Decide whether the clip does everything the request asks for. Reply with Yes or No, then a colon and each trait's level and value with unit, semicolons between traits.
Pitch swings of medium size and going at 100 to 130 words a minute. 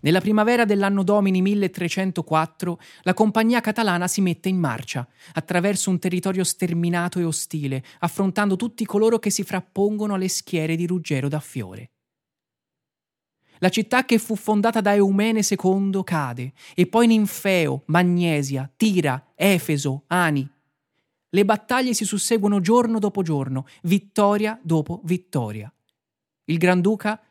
Yes: average, 4.6 semitones; average, 125 wpm